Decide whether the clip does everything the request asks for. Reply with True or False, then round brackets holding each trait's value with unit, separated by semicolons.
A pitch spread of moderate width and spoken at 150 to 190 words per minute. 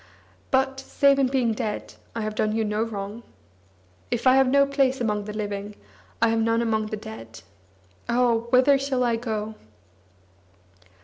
True (3.4 semitones; 165 wpm)